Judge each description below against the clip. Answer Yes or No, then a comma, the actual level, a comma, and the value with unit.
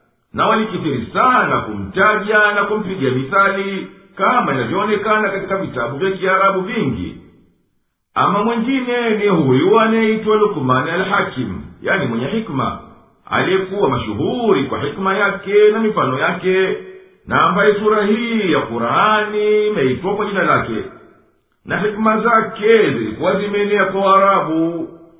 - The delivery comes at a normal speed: Yes, average, 115 wpm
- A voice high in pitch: Yes, high, 200 Hz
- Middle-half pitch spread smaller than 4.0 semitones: Yes, average, 2.9 semitones